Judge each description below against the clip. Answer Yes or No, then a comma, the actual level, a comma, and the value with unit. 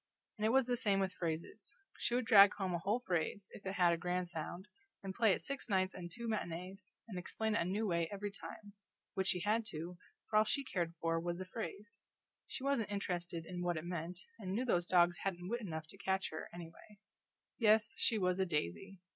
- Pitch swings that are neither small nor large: Yes, average, 3.4 semitones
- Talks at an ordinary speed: No, fast, 220 wpm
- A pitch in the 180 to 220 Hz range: Yes, high, 190 Hz